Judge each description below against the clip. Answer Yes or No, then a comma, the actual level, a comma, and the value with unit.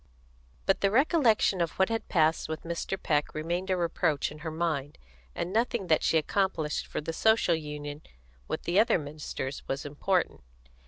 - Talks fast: No, average, 170 wpm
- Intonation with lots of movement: No, average, 4.1 semitones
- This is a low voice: No, medium, 165 Hz